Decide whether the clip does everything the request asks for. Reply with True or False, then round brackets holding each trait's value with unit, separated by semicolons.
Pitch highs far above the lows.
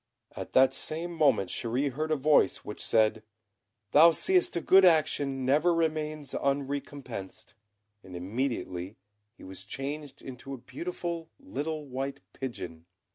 False (4.7 semitones)